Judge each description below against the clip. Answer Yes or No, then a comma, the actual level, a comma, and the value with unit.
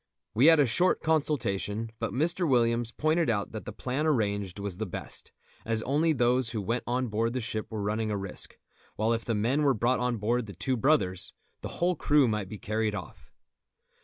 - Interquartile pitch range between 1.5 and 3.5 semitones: No, average, 4.2 semitones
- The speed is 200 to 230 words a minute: Yes, fast, 205 wpm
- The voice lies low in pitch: Yes, low, 115 Hz